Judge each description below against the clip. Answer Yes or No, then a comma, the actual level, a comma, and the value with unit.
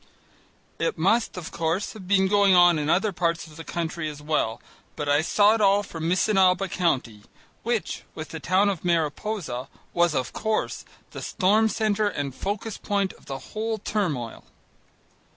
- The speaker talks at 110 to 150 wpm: No, average, 170 wpm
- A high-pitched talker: No, medium, 180 Hz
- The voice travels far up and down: No, average, 4.7 semitones